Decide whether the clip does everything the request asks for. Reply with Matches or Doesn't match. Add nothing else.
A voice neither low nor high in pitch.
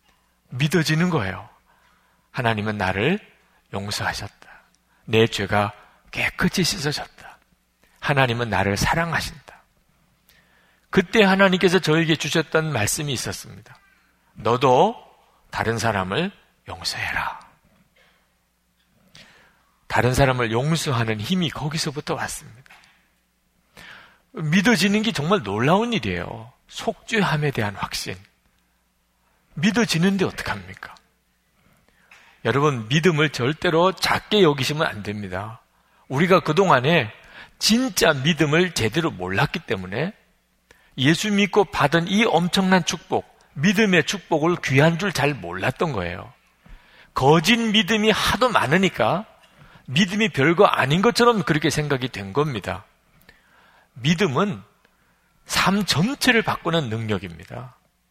Matches